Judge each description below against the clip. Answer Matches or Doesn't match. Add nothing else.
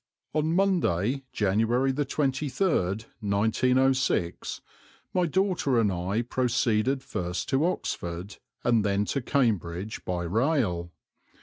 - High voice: Doesn't match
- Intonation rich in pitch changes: Matches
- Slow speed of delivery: Matches